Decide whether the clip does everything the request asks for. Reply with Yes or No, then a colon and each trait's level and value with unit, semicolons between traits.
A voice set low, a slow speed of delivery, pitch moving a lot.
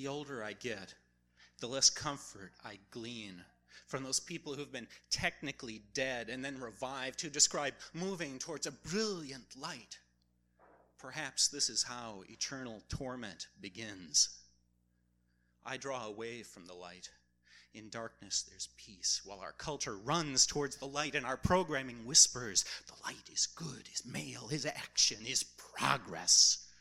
No: low, 120 Hz; average, 145 wpm; wide, 7.5 semitones